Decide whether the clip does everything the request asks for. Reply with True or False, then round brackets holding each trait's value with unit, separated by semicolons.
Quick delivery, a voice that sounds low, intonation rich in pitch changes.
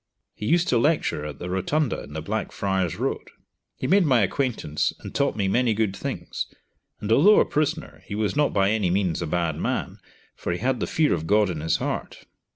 True (210 wpm; 105 Hz; 7.1 semitones)